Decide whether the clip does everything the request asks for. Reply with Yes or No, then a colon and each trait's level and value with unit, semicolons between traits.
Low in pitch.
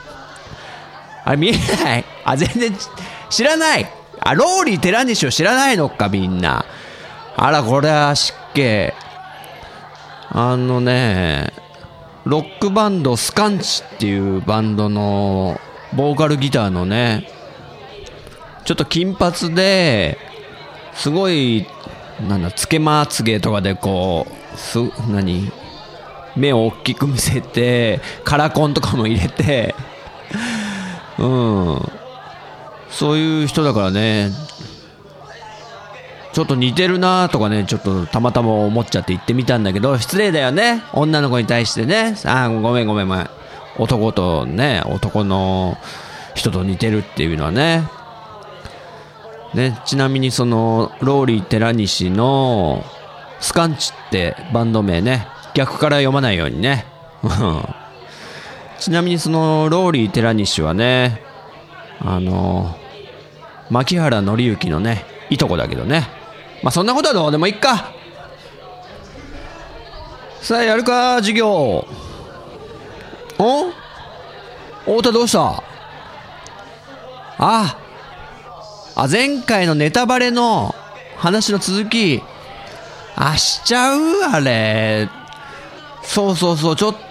Yes: low, 130 Hz